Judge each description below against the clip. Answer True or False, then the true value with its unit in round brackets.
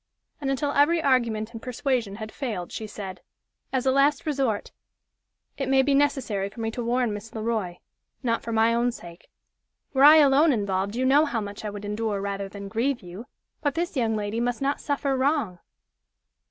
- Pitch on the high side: True (235 Hz)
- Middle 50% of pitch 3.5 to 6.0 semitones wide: True (4.7 semitones)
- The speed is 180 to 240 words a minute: True (195 wpm)